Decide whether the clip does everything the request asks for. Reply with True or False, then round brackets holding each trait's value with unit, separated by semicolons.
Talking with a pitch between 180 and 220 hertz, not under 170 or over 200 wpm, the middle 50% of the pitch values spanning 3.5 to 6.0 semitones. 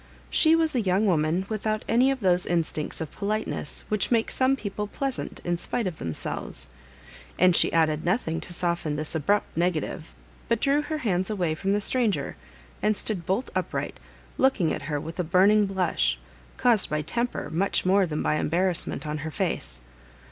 True (185 Hz; 180 wpm; 5.1 semitones)